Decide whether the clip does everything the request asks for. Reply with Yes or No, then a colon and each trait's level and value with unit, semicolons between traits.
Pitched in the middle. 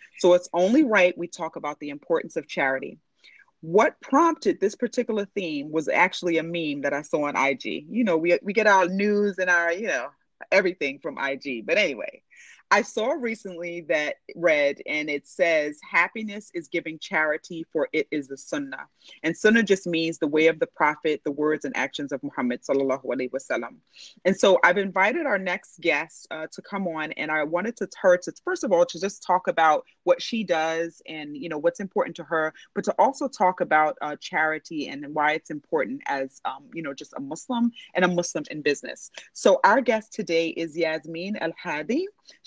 Yes: medium, 170 Hz